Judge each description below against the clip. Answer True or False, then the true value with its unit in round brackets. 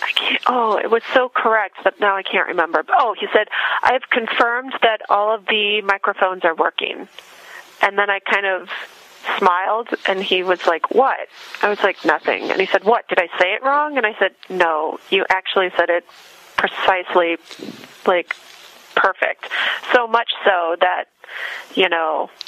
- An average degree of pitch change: True (3.2 semitones)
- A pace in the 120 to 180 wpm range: True (175 wpm)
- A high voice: True (200 Hz)